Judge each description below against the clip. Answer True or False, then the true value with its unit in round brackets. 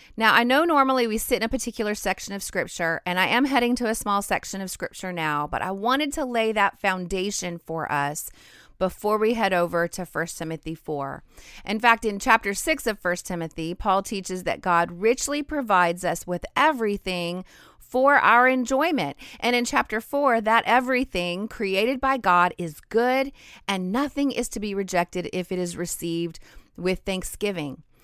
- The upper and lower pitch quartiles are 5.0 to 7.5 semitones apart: True (5.3 semitones)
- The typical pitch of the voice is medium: False (200 Hz)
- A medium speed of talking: True (180 wpm)